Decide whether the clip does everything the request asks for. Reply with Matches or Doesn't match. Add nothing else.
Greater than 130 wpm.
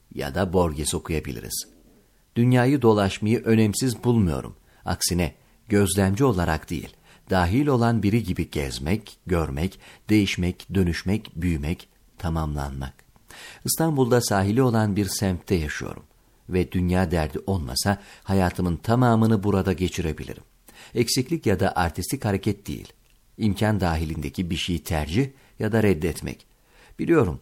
Doesn't match